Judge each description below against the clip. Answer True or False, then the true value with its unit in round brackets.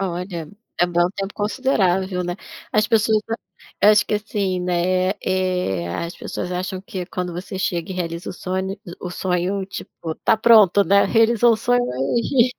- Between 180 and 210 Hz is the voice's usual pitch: True (185 Hz)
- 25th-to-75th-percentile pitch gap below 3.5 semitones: True (2.9 semitones)